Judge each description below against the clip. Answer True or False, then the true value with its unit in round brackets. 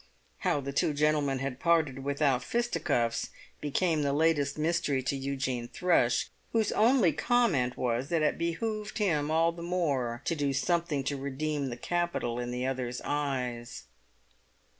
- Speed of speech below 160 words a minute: True (150 wpm)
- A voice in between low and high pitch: True (145 Hz)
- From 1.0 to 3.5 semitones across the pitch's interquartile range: False (4.3 semitones)